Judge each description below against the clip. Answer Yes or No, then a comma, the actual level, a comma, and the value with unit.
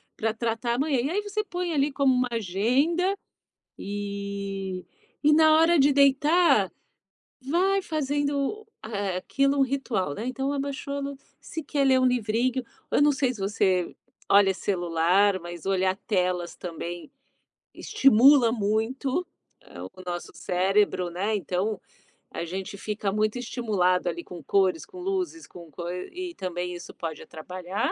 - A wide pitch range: Yes, wide, 7.1 semitones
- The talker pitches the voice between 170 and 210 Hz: No, high, 220 Hz